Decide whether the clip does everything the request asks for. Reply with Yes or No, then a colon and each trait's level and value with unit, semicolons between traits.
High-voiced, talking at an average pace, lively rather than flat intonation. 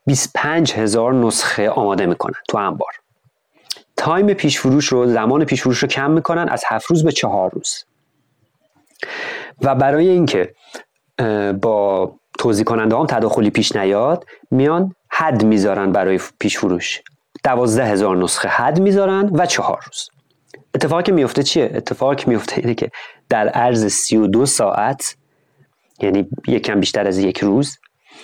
No: low, 135 Hz; average, 140 wpm; wide, 7.0 semitones